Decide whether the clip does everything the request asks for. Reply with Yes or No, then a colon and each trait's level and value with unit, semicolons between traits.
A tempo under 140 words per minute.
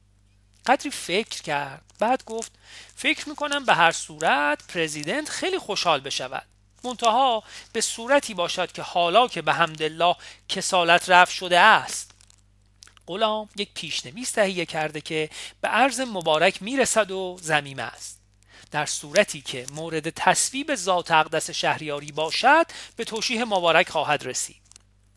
Yes: average, 130 wpm